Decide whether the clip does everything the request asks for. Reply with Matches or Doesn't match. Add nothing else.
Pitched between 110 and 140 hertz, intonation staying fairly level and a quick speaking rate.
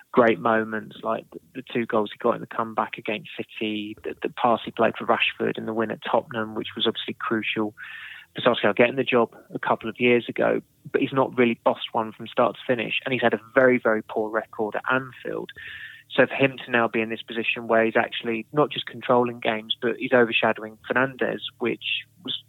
Matches